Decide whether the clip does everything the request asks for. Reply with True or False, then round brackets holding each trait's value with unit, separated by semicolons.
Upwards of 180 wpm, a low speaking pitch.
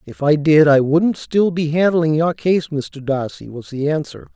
False (205 wpm; 155 Hz)